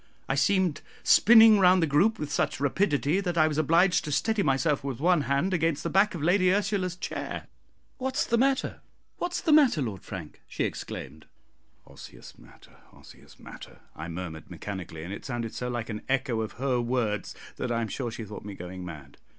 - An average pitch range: No, wide, 8.6 semitones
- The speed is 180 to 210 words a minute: Yes, average, 190 wpm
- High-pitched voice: No, medium, 145 Hz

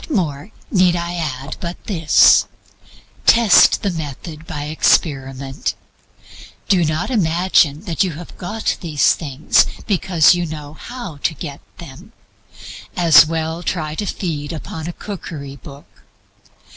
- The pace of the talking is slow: Yes, slow, 130 wpm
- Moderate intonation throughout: Yes, average, 3.3 semitones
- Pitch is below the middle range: No, medium, 160 Hz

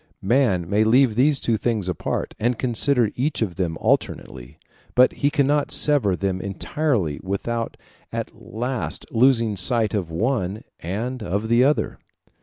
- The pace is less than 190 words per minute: Yes, average, 145 wpm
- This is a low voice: Yes, low, 115 Hz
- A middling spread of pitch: Yes, average, 4.9 semitones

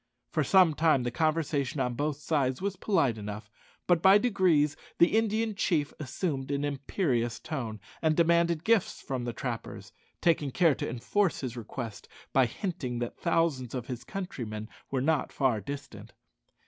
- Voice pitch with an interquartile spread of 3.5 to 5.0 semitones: No, wide, 5.6 semitones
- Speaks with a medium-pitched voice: Yes, medium, 145 Hz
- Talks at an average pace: Yes, average, 160 wpm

